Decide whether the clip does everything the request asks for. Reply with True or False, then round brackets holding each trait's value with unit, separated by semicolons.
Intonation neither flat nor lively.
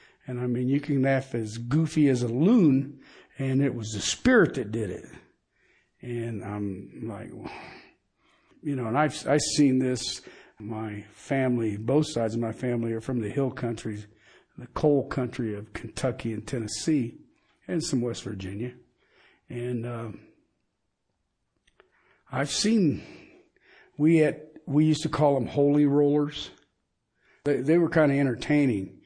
True (4.2 semitones)